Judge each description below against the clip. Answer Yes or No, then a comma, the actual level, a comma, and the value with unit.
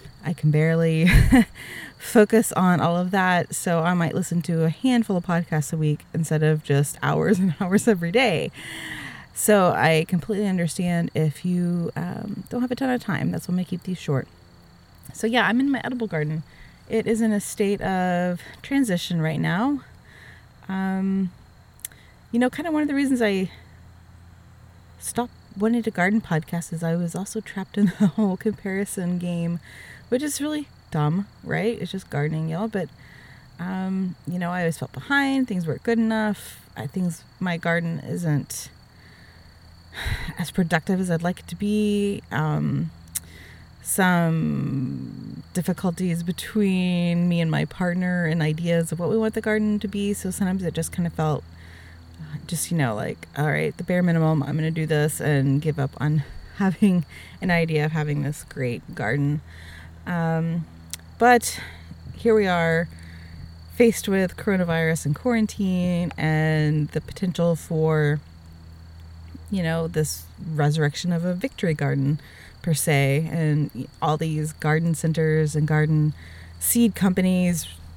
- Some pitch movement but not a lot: Yes, average, 4.2 semitones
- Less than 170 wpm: Yes, average, 160 wpm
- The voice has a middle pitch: Yes, medium, 170 Hz